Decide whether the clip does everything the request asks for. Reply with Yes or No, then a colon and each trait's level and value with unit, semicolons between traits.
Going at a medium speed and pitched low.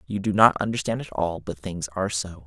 No: fast, 220 wpm; very low, 95 Hz